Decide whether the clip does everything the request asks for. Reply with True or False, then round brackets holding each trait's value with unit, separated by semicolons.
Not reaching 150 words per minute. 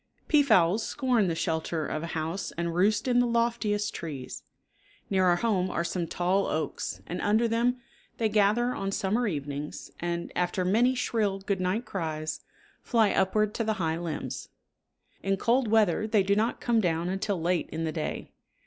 False (175 wpm)